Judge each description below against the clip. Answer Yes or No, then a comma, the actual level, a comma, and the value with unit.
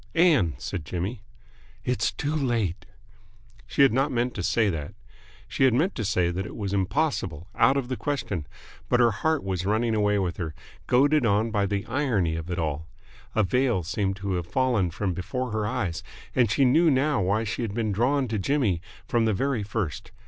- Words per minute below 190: No, average, 200 wpm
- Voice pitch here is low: Yes, low, 110 Hz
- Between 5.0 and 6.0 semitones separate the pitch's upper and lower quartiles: Yes, wide, 5.6 semitones